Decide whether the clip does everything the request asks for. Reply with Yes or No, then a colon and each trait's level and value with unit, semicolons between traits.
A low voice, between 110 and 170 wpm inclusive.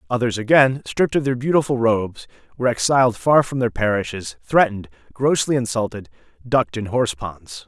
Yes: low, 120 Hz; average, 155 wpm